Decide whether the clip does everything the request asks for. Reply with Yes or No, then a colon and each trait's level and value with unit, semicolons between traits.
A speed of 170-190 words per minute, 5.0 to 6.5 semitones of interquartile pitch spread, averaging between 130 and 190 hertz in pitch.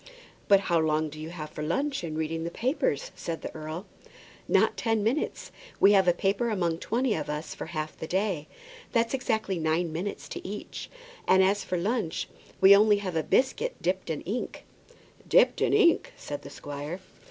Yes: average, 185 wpm; wide, 5.4 semitones; medium, 185 Hz